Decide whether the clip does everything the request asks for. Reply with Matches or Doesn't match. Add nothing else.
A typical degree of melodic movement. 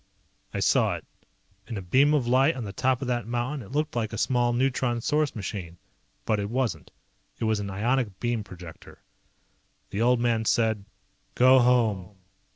Matches